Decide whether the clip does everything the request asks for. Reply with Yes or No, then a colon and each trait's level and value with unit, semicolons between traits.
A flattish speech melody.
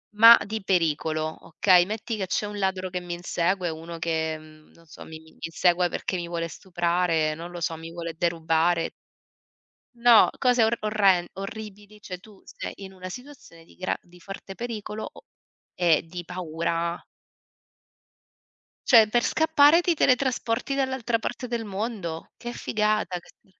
No: average, 4.5 semitones